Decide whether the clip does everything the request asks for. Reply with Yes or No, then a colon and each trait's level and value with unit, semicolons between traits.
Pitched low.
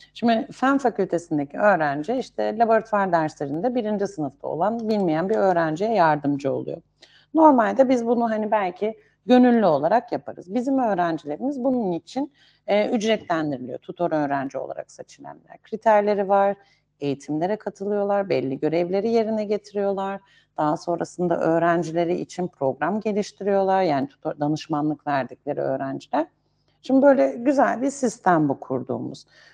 No: high, 195 Hz